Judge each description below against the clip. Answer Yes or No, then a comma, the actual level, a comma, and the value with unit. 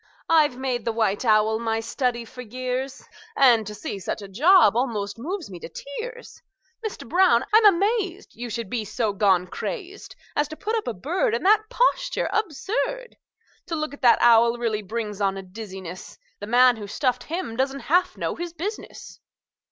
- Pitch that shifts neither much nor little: No, wide, 8.1 semitones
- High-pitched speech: Yes, very high, 250 Hz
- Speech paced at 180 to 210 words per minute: Yes, average, 185 wpm